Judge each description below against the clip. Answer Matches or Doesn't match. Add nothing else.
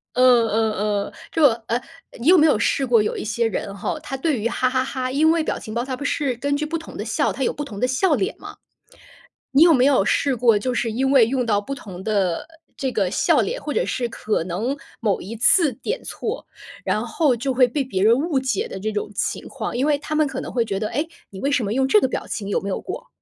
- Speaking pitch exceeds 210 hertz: Matches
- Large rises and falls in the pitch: Doesn't match